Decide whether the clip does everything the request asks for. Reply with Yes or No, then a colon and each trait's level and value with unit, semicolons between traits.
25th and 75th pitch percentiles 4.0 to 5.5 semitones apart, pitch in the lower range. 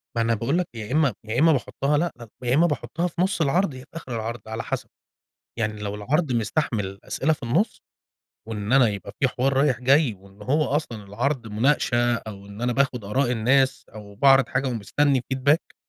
Yes: average, 4.6 semitones; low, 125 Hz